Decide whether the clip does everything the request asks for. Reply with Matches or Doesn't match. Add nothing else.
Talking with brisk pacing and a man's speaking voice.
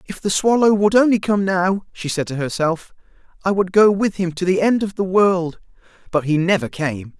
Matches